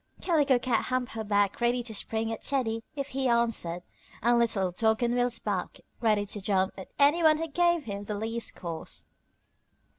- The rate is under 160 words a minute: No, average, 185 wpm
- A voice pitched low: No, high, 230 Hz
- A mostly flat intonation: No, average, 3.8 semitones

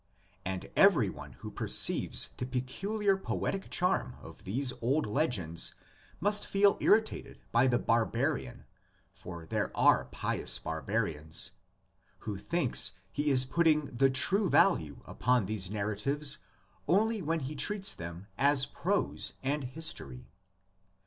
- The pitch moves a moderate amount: No, wide, 8.2 semitones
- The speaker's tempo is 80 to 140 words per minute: Yes, slow, 135 wpm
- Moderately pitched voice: No, low, 130 Hz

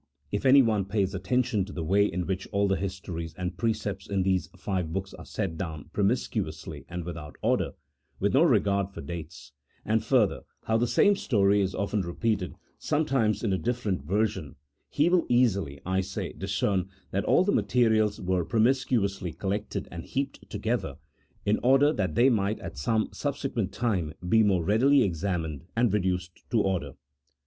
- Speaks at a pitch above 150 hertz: No, low, 100 Hz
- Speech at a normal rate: Yes, average, 175 wpm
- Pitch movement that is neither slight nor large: Yes, average, 3.8 semitones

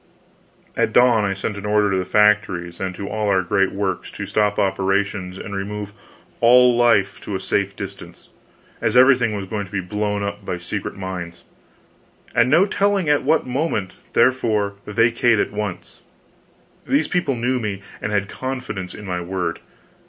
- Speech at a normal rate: Yes, average, 170 wpm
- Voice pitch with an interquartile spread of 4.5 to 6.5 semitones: No, average, 3.7 semitones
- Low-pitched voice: Yes, low, 105 Hz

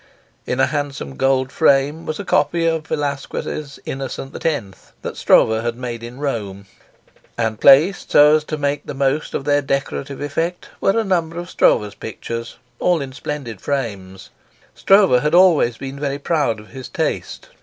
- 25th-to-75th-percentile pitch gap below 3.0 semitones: No, average, 4.2 semitones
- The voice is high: No, medium, 140 Hz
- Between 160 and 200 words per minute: Yes, average, 165 wpm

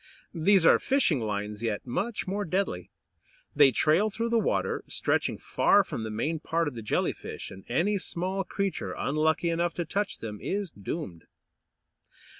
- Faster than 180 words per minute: No, average, 165 wpm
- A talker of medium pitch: Yes, medium, 165 Hz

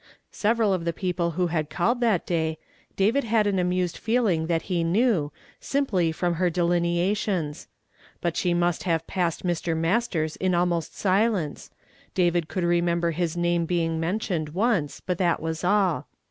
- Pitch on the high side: No, medium, 175 Hz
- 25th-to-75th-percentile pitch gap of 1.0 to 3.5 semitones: Yes, narrow, 2.6 semitones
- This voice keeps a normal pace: Yes, average, 170 wpm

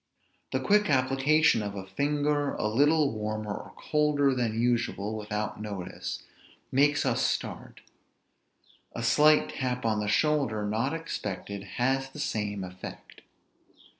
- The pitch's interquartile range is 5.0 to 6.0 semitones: Yes, wide, 5.5 semitones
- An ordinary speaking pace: No, slow, 130 wpm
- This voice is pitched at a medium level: No, low, 120 Hz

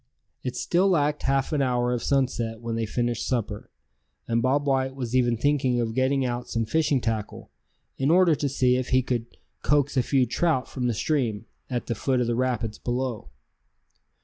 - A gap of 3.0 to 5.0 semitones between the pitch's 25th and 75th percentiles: No, narrow, 2.6 semitones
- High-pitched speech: No, low, 125 Hz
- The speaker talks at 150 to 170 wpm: No, average, 190 wpm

